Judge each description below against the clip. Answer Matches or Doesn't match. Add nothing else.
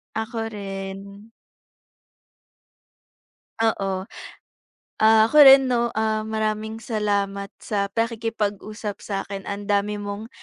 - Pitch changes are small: Matches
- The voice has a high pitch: Matches